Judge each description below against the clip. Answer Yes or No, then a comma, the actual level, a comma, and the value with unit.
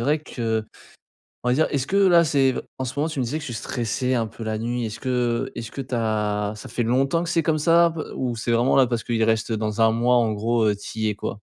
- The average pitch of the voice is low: Yes, low, 120 Hz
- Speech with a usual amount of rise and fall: Yes, average, 3.5 semitones